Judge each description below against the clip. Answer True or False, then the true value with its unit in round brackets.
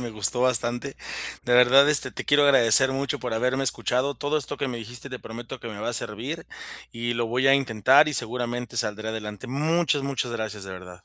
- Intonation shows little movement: False (3.3 semitones)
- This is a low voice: True (125 Hz)